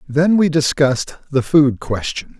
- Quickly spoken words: No, average, 150 wpm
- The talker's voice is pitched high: No, medium, 150 Hz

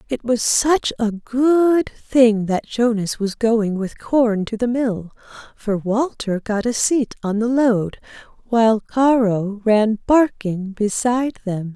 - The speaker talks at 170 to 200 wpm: No, average, 150 wpm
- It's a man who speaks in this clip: No, female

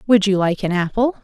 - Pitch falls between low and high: No, high, 205 Hz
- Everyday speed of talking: No, fast, 245 wpm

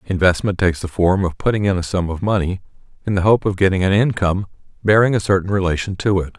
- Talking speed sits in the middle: No, fast, 225 wpm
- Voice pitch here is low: Yes, very low, 95 Hz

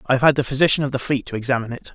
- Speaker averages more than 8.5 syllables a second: Yes, 8.7 syllables/s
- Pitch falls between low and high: No, low, 130 Hz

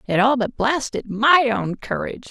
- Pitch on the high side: Yes, high, 220 Hz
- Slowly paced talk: No, average, 180 wpm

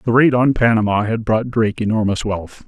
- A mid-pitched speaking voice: No, low, 110 Hz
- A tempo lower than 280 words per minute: Yes, average, 200 wpm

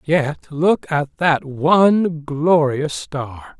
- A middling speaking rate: No, slow, 115 wpm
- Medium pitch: Yes, medium, 150 Hz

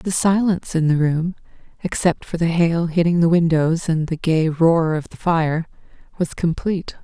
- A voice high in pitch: No, medium, 165 Hz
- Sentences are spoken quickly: No, average, 180 wpm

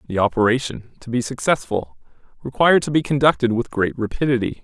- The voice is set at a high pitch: No, low, 125 Hz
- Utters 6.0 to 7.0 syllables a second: Yes, 6.1 syllables/s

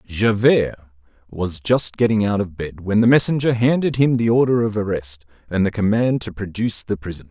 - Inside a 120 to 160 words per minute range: No, average, 190 wpm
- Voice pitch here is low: Yes, low, 105 Hz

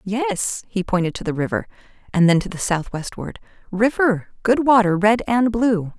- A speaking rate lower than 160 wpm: Yes, average, 150 wpm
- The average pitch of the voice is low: No, high, 200 Hz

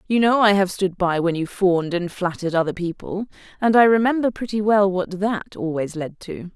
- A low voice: No, high, 190 Hz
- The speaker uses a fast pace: Yes, fast, 210 wpm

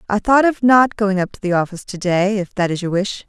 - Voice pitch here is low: No, high, 200 Hz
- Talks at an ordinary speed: No, fast, 275 wpm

